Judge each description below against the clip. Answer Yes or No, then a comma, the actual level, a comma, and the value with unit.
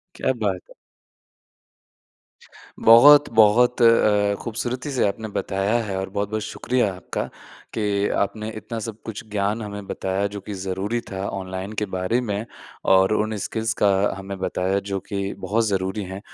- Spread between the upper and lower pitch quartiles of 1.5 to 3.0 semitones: Yes, narrow, 2.4 semitones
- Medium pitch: No, low, 105 Hz